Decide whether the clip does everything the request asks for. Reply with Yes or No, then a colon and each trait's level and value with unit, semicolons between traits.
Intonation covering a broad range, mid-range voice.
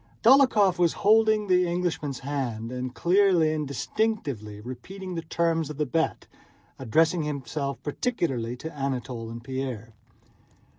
Yes: wide, 5.9 semitones; medium, 150 Hz